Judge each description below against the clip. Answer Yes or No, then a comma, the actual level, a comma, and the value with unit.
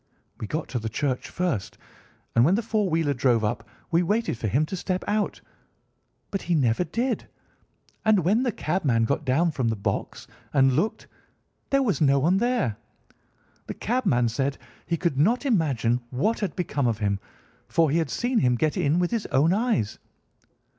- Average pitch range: No, wide, 8.0 semitones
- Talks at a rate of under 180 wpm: No, average, 185 wpm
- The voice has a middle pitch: Yes, medium, 155 Hz